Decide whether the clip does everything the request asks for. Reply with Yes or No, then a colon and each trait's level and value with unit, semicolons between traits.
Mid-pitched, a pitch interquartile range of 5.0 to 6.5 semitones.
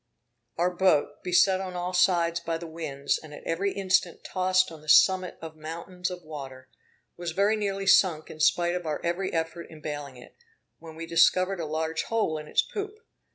No: medium, 170 Hz; average, 2.8 semitones